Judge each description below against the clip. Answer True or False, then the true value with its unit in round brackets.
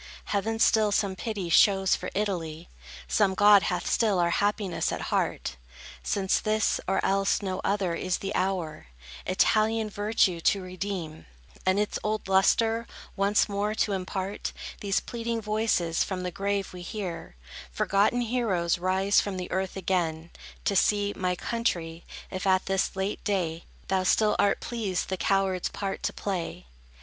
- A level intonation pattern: True (2.2 semitones)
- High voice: True (195 Hz)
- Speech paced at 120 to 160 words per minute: True (150 wpm)